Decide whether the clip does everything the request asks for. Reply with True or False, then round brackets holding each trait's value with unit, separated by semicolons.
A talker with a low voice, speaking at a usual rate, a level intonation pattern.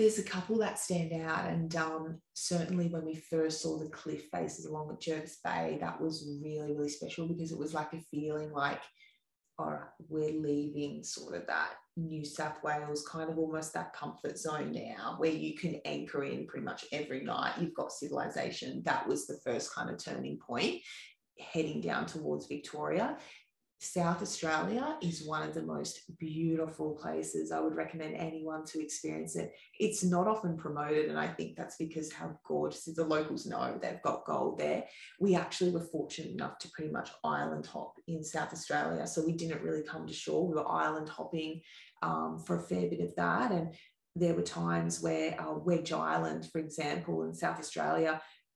False (155 Hz; 190 wpm; 2.1 semitones)